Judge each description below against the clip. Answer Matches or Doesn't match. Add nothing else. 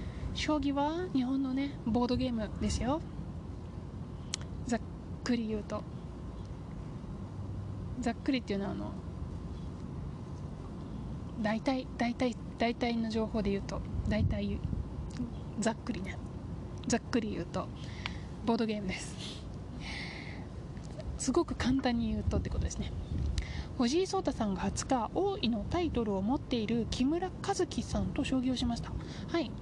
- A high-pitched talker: Matches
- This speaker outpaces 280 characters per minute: Doesn't match